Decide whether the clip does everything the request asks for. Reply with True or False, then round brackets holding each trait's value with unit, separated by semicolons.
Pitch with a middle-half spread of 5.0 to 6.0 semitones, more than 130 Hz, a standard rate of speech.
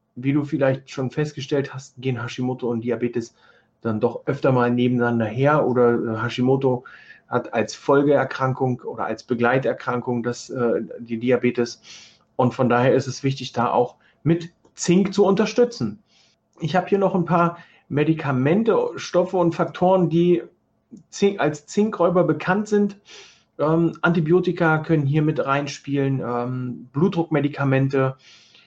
True (5.3 semitones; 140 Hz; 135 wpm)